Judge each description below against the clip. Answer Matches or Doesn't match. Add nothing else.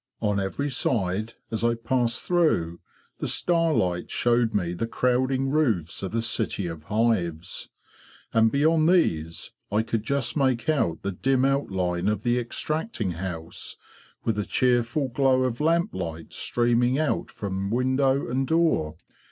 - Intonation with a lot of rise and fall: Matches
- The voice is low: Matches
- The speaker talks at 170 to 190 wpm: Doesn't match